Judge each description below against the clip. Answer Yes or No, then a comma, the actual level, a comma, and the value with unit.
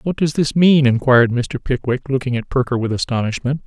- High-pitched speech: No, low, 130 Hz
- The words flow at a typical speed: Yes, average, 195 wpm